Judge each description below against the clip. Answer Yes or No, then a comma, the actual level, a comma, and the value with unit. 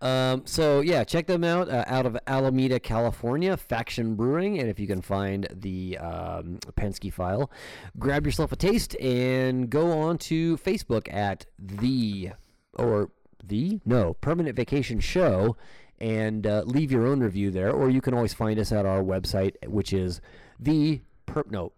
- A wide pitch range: Yes, wide, 6.0 semitones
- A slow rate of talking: No, average, 165 wpm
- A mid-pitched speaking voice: No, low, 120 Hz